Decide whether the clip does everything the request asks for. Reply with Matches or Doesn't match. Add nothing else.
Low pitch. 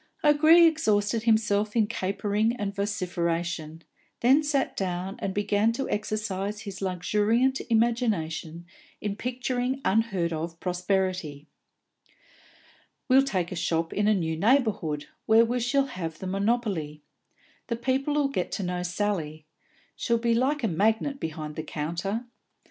Doesn't match